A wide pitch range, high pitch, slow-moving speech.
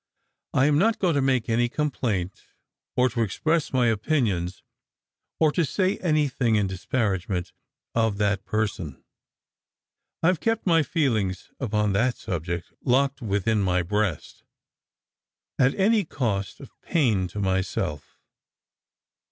No: wide, 6.5 semitones; low, 115 Hz; slow, 125 wpm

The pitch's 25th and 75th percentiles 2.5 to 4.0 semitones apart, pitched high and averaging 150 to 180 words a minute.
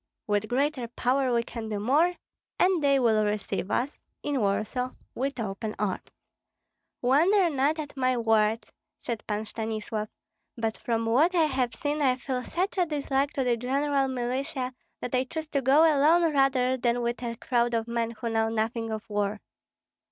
Yes: average, 3.7 semitones; very high, 250 Hz; average, 175 wpm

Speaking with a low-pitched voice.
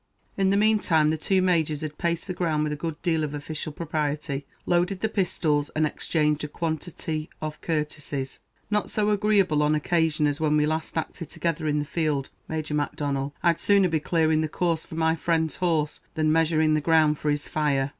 No: medium, 155 Hz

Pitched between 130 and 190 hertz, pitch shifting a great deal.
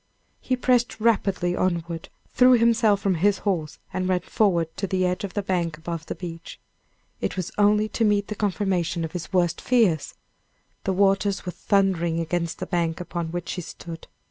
No: medium, 185 Hz; average, 3.2 semitones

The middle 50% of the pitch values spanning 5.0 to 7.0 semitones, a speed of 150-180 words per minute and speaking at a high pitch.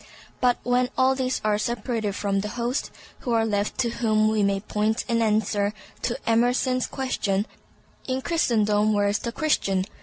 No: average, 3.1 semitones; average, 170 wpm; high, 225 Hz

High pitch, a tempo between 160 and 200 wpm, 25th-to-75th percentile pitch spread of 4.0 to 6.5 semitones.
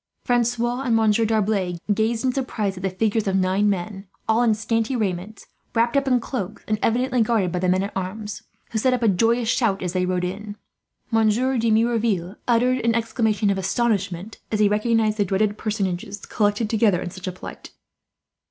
No: high, 215 Hz; average, 190 wpm; average, 3.0 semitones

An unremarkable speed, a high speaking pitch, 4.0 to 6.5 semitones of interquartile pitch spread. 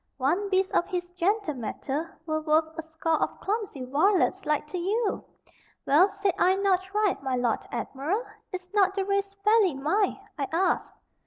Yes: average, 170 wpm; very high, 360 Hz; average, 4.3 semitones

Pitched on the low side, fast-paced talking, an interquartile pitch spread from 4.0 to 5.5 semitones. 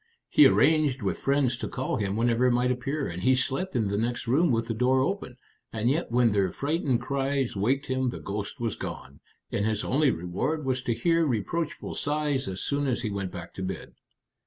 Yes: low, 125 Hz; fast, 210 wpm; average, 4.4 semitones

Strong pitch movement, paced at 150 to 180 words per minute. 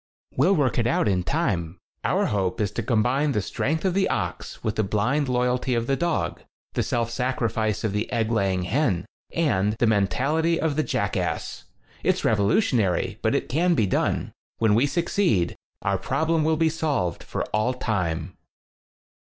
Yes: wide, 6.5 semitones; average, 170 wpm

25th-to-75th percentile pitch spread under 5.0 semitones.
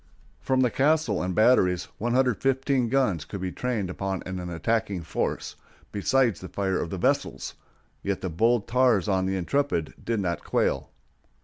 No: wide, 5.4 semitones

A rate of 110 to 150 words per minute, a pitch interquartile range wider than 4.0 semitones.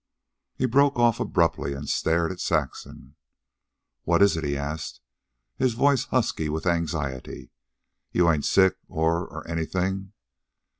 Yes: slow, 135 wpm; average, 4.7 semitones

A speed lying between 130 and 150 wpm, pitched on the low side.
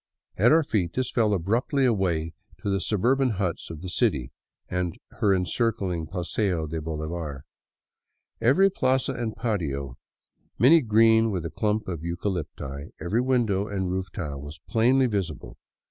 Yes: average, 145 wpm; very low, 95 Hz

